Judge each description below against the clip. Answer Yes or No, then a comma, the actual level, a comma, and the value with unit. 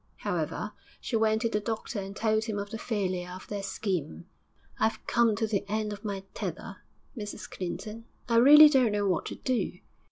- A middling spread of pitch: No, narrow, 2.3 semitones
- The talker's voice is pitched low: No, high, 215 Hz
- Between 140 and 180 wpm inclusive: No, average, 190 wpm